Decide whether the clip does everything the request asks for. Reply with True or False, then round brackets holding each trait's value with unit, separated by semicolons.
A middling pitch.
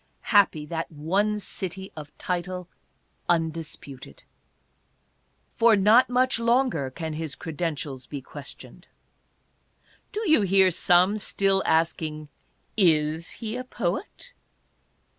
True (175 Hz)